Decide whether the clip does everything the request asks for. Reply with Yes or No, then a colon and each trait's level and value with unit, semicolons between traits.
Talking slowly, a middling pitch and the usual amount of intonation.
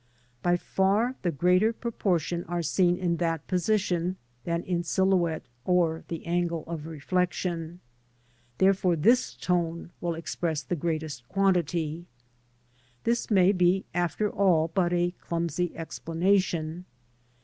No: slow, 120 wpm; medium, 175 Hz; narrow, 2.1 semitones